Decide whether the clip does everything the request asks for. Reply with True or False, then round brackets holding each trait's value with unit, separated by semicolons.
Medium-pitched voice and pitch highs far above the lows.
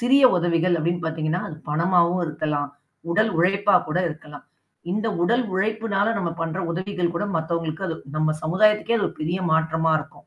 False (170 Hz; 3.7 semitones)